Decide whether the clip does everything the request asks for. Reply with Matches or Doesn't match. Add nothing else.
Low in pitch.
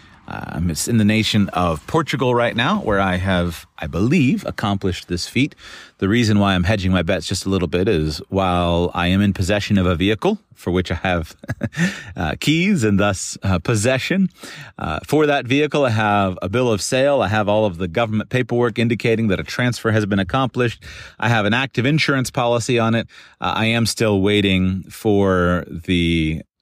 Matches